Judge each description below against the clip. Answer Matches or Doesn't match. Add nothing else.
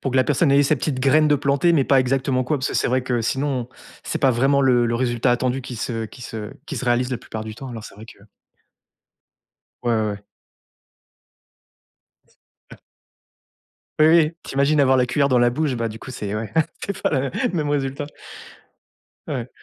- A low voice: Matches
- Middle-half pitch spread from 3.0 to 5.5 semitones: Doesn't match